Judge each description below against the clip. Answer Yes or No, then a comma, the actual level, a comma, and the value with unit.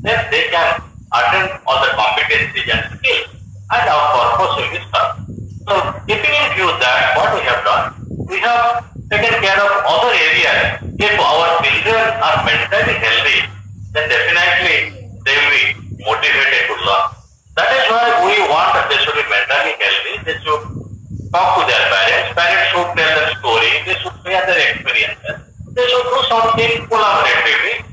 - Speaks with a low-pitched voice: No, high, 210 Hz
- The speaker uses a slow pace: No, average, 165 wpm